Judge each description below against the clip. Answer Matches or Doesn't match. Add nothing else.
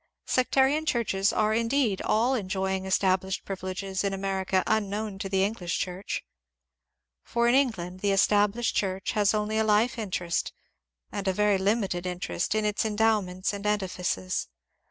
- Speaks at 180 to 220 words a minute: Doesn't match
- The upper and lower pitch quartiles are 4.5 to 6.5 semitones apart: Doesn't match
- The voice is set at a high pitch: Matches